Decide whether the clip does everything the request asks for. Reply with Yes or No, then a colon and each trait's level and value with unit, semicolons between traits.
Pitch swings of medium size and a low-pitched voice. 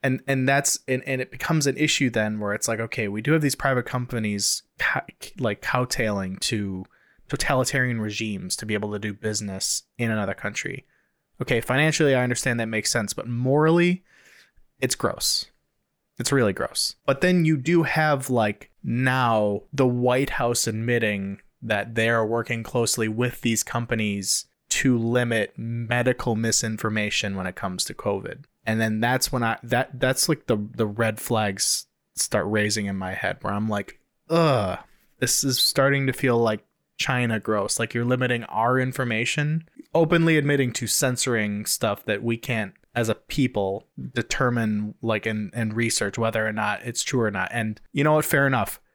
Yes: average, 3.3 semitones; low, 115 Hz